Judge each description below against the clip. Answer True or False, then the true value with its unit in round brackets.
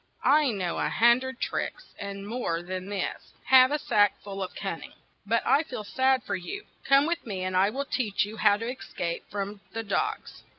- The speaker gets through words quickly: True (215 wpm)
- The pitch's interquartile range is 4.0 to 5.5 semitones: True (4.9 semitones)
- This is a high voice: True (215 Hz)